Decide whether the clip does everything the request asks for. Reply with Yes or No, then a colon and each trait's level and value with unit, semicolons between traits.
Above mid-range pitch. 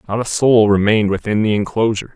No: low, 110 Hz